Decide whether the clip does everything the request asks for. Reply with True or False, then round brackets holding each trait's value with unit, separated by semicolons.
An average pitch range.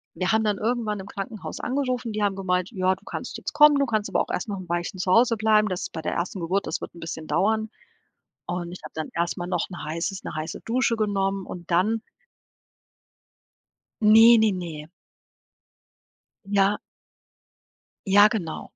True (3.4 semitones)